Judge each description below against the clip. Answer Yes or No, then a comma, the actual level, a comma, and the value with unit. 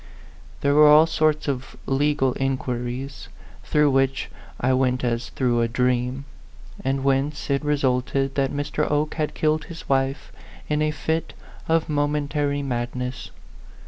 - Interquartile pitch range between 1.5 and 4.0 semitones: Yes, narrow, 2.6 semitones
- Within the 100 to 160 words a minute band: Yes, average, 145 wpm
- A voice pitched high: No, low, 135 Hz